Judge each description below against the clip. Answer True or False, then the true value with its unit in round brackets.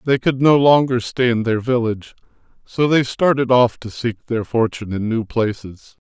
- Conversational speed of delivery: True (185 wpm)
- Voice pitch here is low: True (120 Hz)